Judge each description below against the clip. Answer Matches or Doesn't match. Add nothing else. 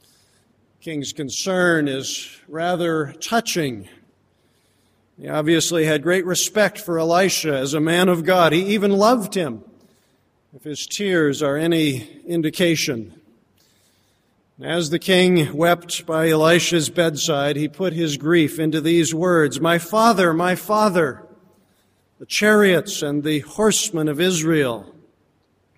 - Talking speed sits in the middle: Doesn't match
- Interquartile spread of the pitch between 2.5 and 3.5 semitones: Matches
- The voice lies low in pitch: Doesn't match